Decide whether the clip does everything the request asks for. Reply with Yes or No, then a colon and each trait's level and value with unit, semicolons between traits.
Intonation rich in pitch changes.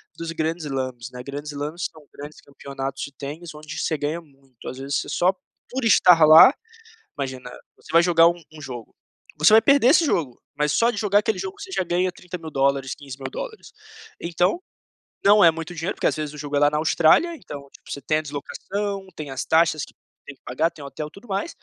No: average, 4.3 semitones